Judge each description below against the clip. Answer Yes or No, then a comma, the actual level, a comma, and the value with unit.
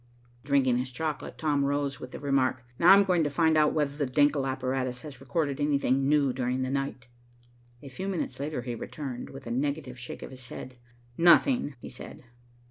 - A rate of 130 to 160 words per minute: No, average, 195 wpm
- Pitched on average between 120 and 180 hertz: Yes, medium, 140 Hz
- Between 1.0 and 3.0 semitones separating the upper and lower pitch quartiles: Yes, narrow, 2.6 semitones